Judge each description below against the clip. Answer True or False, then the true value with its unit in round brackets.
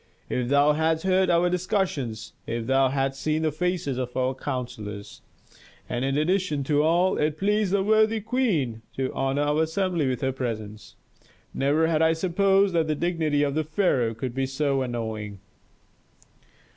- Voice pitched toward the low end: False (150 Hz)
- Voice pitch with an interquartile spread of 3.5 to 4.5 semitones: False (5.3 semitones)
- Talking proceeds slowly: False (160 wpm)